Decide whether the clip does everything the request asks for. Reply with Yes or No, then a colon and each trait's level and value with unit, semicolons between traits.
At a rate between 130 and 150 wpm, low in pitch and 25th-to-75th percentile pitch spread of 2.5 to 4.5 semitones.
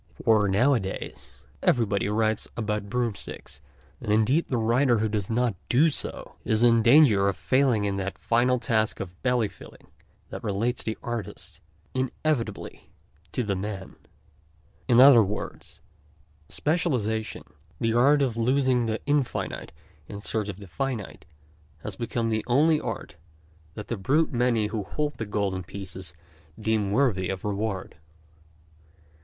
Yes: average, 140 wpm; low, 110 Hz; average, 3.5 semitones